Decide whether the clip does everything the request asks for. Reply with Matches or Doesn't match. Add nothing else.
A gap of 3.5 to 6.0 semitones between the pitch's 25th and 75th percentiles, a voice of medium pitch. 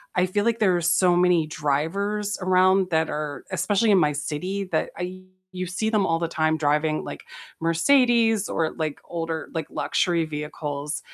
Matches